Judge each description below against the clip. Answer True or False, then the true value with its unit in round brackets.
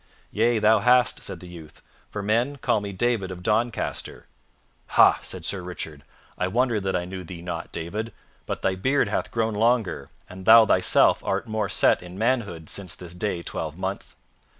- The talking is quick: False (175 wpm)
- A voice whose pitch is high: False (100 Hz)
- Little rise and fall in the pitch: False (4.1 semitones)